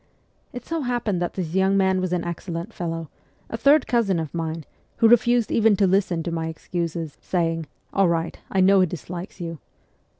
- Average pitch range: Yes, average, 3.3 semitones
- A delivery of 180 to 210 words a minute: Yes, average, 195 wpm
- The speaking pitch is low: No, medium, 180 Hz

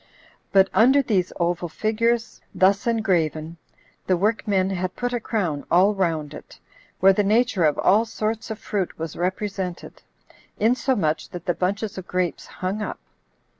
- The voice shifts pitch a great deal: No, average, 3.8 semitones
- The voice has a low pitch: No, high, 195 Hz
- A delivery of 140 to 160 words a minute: Yes, average, 150 wpm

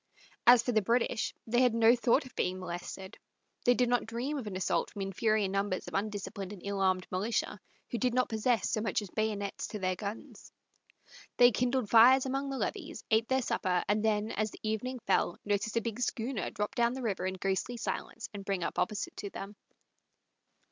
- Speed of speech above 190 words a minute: Yes, fast, 205 wpm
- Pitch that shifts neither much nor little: Yes, average, 3.5 semitones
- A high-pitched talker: Yes, high, 220 Hz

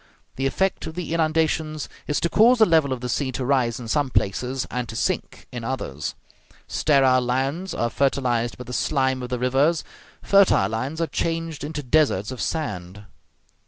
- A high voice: No, low, 135 Hz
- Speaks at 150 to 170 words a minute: No, average, 180 wpm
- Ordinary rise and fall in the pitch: Yes, average, 4.3 semitones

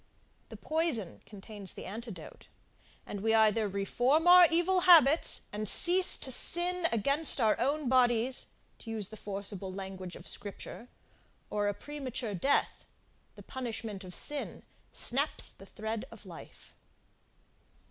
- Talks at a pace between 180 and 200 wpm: No, slow, 135 wpm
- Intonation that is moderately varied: No, wide, 6.3 semitones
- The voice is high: Yes, high, 230 Hz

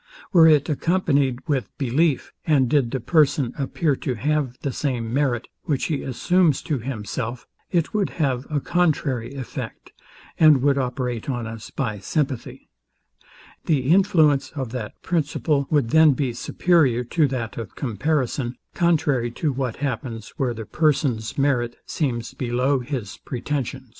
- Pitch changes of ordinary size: Yes, average, 3.7 semitones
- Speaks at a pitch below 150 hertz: Yes, low, 135 Hz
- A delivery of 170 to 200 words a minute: No, average, 155 wpm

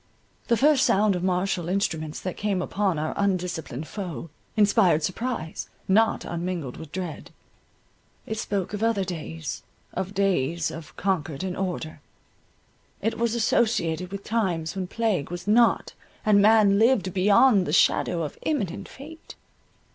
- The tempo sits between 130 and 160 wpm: Yes, average, 140 wpm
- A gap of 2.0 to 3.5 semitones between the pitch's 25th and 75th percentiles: No, average, 4.1 semitones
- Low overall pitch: No, high, 190 Hz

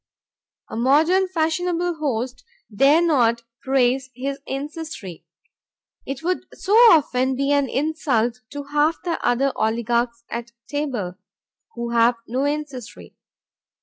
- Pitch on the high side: Yes, very high, 270 Hz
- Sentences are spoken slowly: Yes, slow, 115 wpm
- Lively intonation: No, average, 4.3 semitones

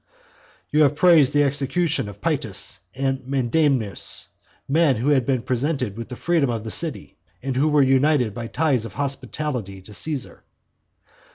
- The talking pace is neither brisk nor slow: Yes, average, 160 wpm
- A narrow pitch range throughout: No, average, 3.8 semitones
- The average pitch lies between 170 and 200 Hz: No, low, 135 Hz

